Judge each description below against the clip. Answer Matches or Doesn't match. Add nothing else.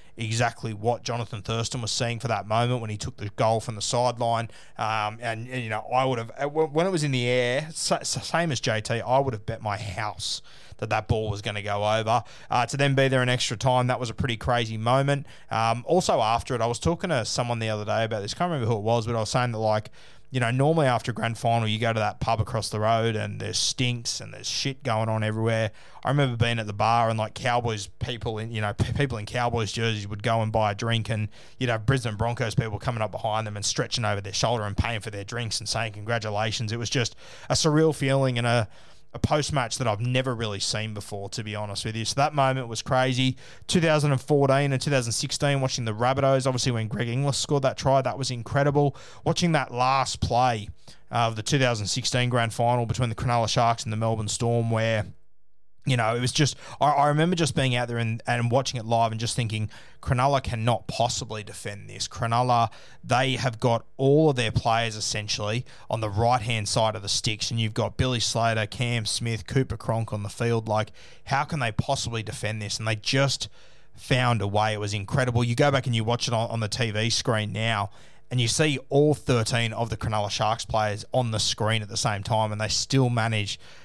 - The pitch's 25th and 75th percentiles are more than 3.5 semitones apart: Doesn't match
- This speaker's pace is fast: Matches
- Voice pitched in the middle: Doesn't match